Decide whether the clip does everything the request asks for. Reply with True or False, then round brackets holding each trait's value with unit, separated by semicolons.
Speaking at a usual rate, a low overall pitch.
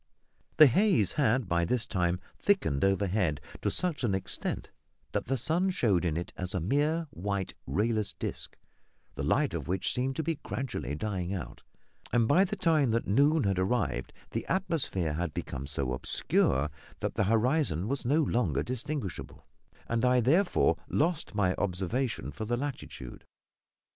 True (160 wpm; 110 Hz)